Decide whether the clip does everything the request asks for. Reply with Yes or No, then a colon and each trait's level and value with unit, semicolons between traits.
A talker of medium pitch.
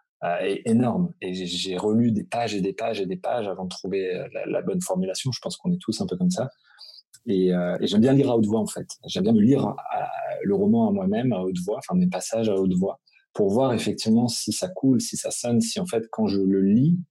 No: low, 130 Hz